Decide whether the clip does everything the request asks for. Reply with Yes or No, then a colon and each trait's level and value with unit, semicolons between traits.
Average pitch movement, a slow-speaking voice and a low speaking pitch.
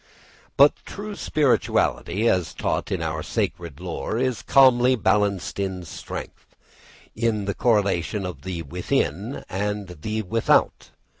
Yes: average, 4.5 semitones; slow, 125 wpm; low, 105 Hz